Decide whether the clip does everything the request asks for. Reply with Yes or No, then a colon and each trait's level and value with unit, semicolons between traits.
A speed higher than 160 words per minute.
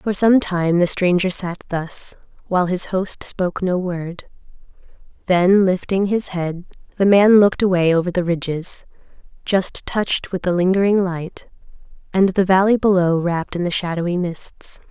No: average, 155 wpm